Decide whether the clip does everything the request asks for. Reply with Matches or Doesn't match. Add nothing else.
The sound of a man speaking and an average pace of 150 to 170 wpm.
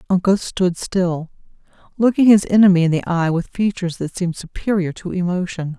Doesn't match